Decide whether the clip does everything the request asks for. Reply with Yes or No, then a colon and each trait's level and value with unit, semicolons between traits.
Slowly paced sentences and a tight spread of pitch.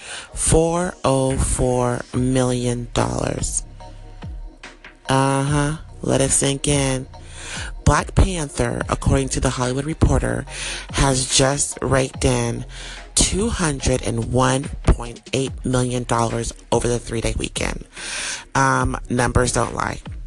Yes: slow, 90 wpm; narrow, 2.2 semitones